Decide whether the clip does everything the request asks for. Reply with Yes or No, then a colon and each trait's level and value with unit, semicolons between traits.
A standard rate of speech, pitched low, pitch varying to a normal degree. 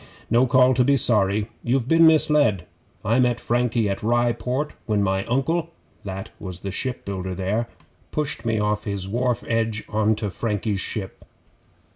Yes: average, 160 wpm; low, 115 Hz; average, 3.8 semitones